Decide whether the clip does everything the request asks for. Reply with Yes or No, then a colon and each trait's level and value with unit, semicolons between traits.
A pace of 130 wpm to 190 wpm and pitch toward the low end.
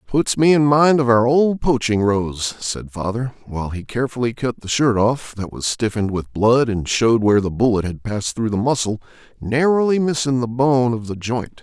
No: fast, 205 wpm; low, 120 Hz